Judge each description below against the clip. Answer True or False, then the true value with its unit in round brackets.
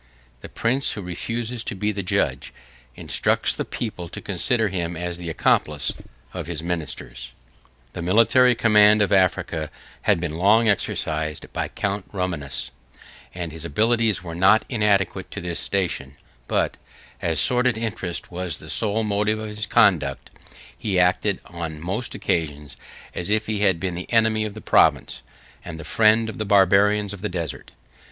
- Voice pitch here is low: True (95 Hz)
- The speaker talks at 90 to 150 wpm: False (160 wpm)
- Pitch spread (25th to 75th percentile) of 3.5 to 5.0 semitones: True (4.1 semitones)